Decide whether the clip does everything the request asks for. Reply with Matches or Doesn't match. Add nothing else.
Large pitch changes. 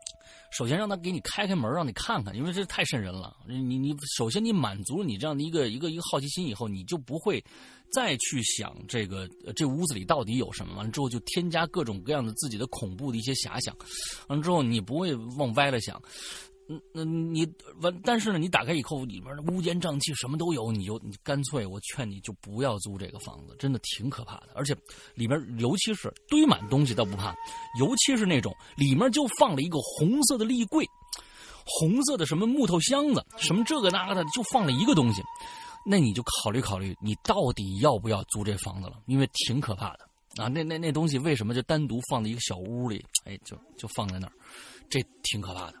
Matches